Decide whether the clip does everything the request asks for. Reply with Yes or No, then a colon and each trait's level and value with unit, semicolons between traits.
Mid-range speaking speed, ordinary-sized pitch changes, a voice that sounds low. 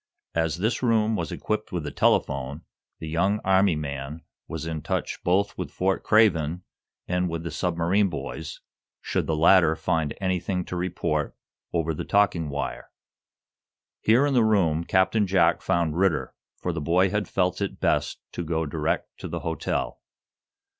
Yes: average, 160 wpm; average, 3.4 semitones; very low, 90 Hz